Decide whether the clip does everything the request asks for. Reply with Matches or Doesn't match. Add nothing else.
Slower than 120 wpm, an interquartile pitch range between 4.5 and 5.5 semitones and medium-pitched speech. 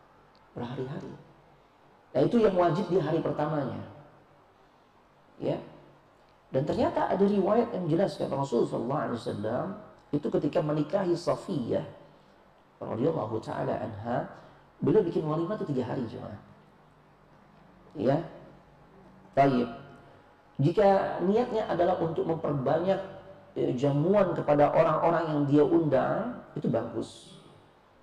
Matches